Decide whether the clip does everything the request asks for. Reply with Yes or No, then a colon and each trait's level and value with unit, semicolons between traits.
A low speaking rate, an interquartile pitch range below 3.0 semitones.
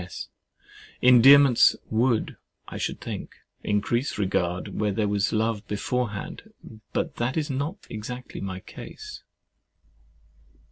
No: slow, 110 wpm; average, 3.7 semitones